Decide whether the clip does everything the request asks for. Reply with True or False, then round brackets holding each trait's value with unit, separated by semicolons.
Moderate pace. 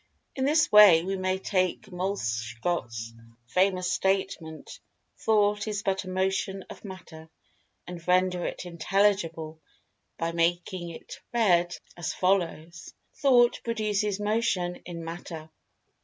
False (115 wpm)